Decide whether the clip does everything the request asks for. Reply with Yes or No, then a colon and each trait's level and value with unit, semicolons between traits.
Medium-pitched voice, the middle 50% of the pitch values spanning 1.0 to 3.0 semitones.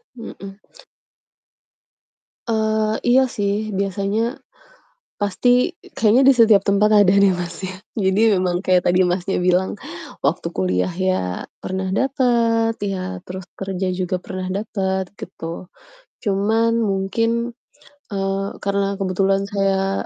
No: high, 195 Hz; average, 2.7 semitones